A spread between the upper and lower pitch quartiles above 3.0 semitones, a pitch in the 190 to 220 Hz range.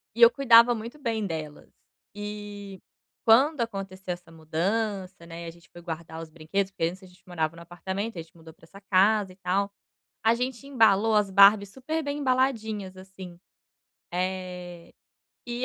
Yes: average, 4.3 semitones; high, 195 Hz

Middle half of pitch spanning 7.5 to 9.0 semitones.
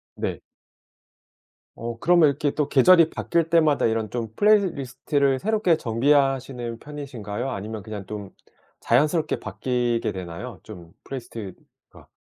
No: average, 5.1 semitones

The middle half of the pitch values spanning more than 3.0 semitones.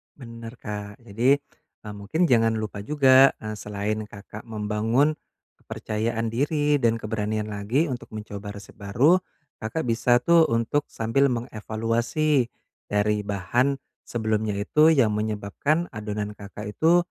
Yes: average, 4.0 semitones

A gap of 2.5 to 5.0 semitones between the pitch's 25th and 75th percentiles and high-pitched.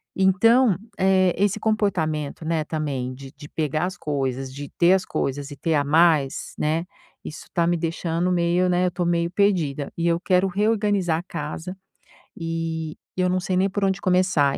No: average, 3.4 semitones; medium, 170 Hz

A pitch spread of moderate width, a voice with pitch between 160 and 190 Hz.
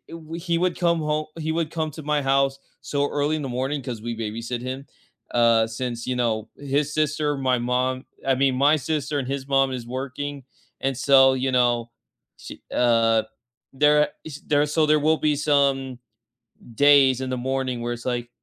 No: average, 3.0 semitones; low, 135 Hz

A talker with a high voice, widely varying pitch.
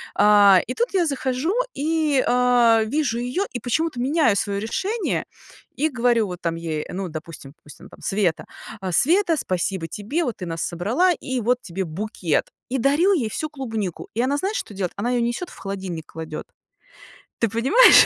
Yes: high, 235 Hz; wide, 7.0 semitones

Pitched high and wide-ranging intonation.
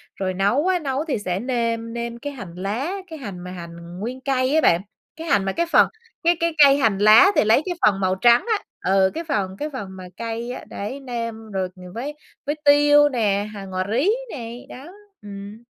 Yes: high, 230 Hz; wide, 6.2 semitones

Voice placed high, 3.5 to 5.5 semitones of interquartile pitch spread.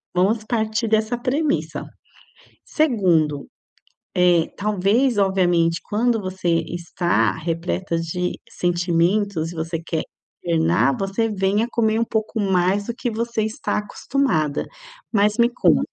Yes: high, 195 Hz; average, 4.4 semitones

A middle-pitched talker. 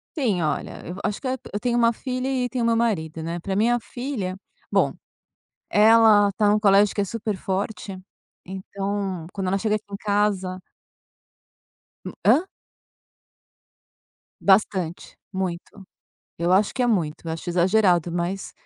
No: high, 200 Hz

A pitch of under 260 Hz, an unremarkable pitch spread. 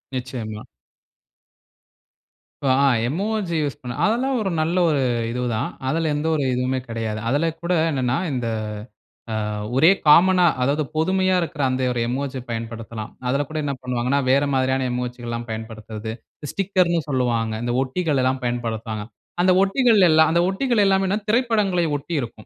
No: low, 135 Hz; wide, 6.4 semitones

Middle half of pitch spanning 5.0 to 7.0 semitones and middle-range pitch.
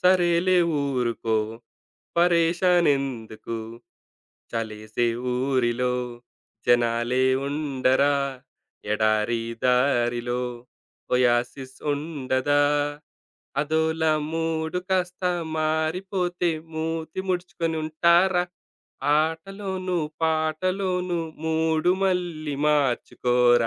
Yes: wide, 5.6 semitones; medium, 155 Hz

